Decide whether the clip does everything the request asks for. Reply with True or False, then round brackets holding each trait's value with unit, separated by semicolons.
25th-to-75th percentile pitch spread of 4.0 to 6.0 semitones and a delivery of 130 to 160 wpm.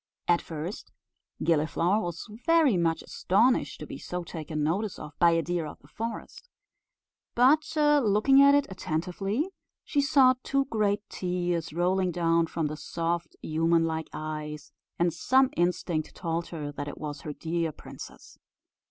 True (5.1 semitones; 150 wpm)